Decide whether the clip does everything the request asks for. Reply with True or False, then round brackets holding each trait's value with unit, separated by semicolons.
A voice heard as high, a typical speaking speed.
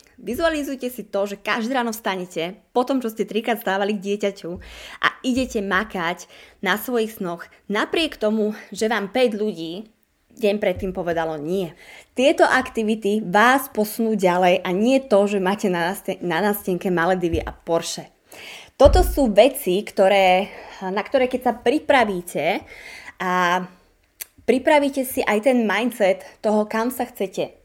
True (210 Hz; 140 wpm)